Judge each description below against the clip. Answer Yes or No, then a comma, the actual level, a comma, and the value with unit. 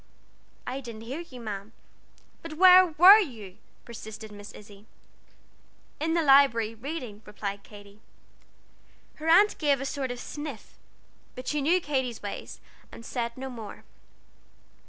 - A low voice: No, very high, 250 Hz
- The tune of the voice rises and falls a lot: Yes, wide, 5.8 semitones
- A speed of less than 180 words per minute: Yes, slow, 135 wpm